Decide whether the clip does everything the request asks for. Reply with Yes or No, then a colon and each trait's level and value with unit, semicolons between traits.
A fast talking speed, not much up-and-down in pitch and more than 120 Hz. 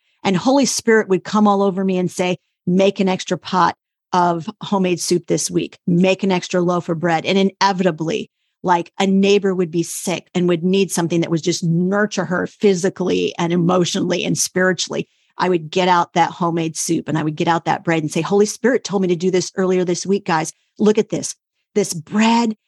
Yes: fast, 210 wpm; narrow, 2.3 semitones; medium, 185 Hz